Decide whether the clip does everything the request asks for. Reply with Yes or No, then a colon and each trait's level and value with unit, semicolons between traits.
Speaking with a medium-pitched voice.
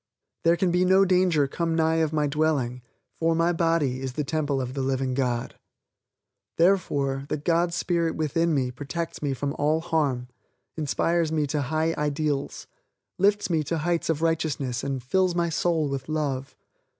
Yes: medium, 155 Hz